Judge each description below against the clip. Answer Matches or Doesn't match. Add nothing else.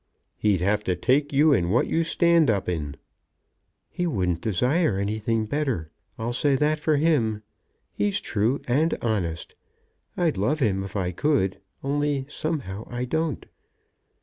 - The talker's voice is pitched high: Doesn't match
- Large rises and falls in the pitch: Matches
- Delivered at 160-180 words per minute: Doesn't match